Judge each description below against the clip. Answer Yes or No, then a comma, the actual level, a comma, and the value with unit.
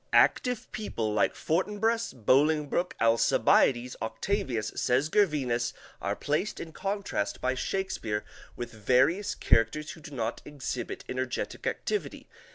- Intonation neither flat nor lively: No, wide, 7.9 semitones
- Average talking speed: No, slow, 120 wpm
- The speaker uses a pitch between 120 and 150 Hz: Yes, low, 135 Hz